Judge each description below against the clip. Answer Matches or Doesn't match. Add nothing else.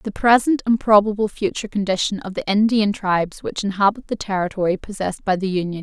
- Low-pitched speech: Doesn't match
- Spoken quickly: Doesn't match